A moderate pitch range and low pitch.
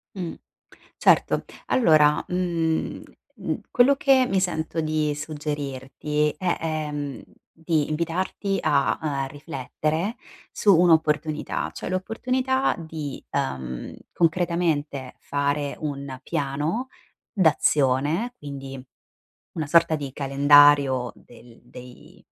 No: average, 3.3 semitones; medium, 150 Hz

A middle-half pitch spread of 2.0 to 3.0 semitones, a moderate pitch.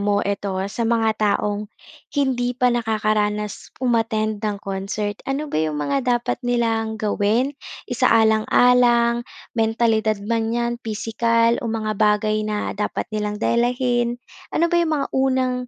No: narrow, 2.4 semitones; high, 225 Hz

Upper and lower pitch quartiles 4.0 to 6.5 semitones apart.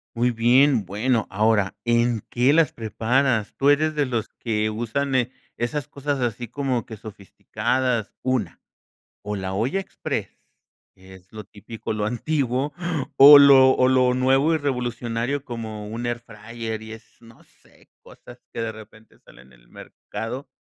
No: average, 3.2 semitones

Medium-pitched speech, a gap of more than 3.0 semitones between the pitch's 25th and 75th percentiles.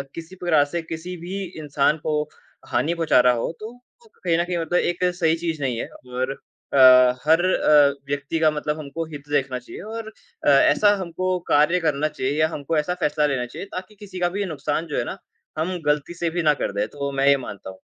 Yes: medium, 155 Hz; average, 3.7 semitones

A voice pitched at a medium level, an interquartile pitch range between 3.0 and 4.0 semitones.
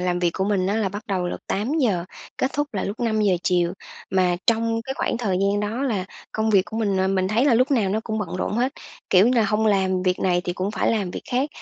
No: high, 205 Hz; average, 3.5 semitones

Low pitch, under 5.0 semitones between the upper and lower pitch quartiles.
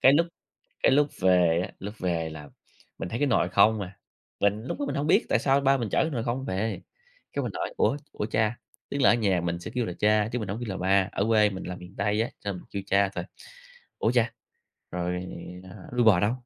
Yes: low, 105 Hz; average, 4.4 semitones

